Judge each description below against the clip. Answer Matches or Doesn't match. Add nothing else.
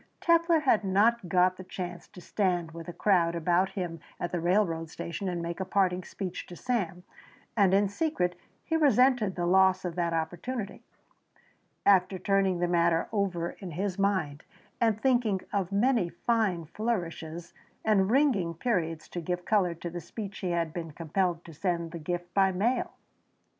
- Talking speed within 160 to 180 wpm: Matches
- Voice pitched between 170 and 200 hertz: Matches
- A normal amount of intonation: Matches